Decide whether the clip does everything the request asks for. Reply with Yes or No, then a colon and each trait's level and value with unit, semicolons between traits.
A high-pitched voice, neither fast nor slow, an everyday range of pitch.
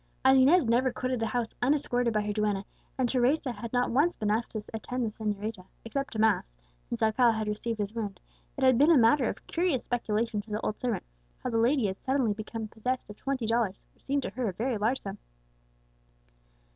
No: high, 230 Hz; fast, 215 wpm; average, 3.3 semitones